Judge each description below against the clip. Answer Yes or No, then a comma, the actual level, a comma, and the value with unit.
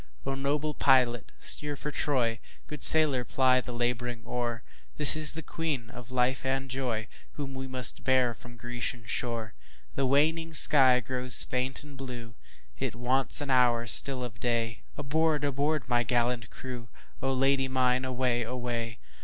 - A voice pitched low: Yes, low, 125 Hz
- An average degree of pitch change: No, narrow, 2.2 semitones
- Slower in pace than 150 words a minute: Yes, slow, 135 wpm